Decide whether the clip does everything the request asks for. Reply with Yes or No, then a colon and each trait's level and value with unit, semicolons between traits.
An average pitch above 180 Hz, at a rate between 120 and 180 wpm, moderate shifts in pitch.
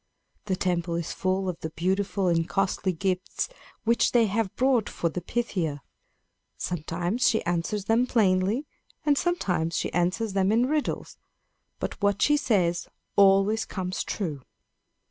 Yes: high, 190 Hz; average, 145 wpm; average, 4.1 semitones